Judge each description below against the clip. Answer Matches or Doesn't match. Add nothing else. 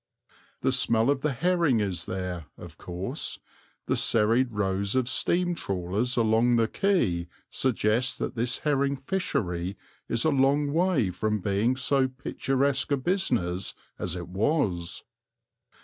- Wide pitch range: Matches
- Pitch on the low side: Matches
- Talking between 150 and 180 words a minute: Doesn't match